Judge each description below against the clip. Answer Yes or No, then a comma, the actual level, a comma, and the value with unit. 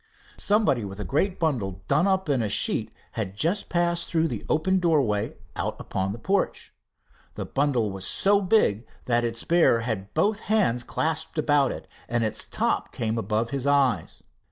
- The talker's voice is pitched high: No, medium, 140 Hz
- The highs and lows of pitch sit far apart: Yes, wide, 7.5 semitones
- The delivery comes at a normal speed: Yes, average, 175 wpm